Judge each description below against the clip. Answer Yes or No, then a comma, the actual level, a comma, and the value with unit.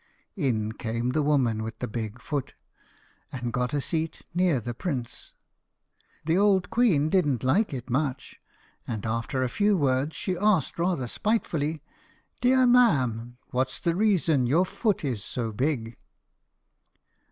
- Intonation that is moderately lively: No, wide, 6.8 semitones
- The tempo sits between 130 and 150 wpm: Yes, average, 140 wpm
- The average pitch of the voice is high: No, medium, 140 Hz